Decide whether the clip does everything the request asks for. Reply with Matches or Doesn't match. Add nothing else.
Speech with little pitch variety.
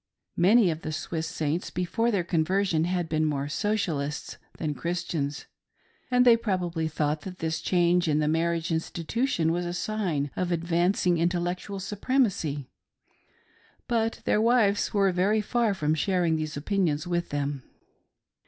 Doesn't match